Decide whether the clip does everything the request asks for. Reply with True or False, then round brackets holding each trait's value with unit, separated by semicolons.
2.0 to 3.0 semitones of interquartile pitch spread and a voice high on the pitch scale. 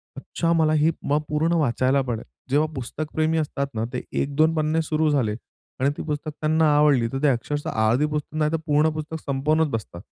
False (2.6 semitones; 150 Hz)